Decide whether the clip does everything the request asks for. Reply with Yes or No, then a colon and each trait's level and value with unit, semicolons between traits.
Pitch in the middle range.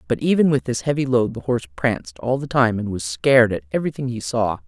No: low, 115 Hz